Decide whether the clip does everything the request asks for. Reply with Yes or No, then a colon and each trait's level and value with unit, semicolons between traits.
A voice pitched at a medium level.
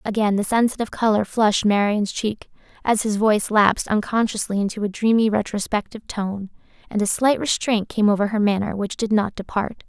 No: high, 210 Hz